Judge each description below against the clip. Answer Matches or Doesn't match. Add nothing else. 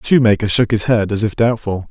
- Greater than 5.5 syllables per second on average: Matches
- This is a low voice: Matches